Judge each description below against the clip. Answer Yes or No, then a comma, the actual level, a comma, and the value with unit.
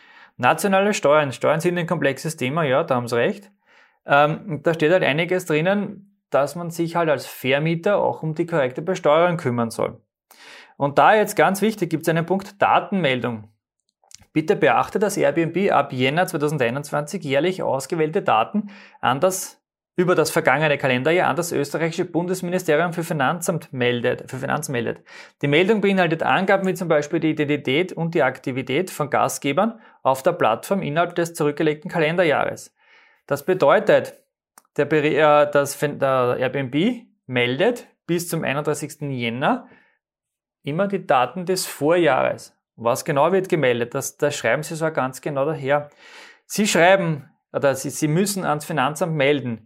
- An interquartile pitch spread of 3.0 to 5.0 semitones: Yes, average, 4.7 semitones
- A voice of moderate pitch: Yes, medium, 165 Hz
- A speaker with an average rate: Yes, average, 150 wpm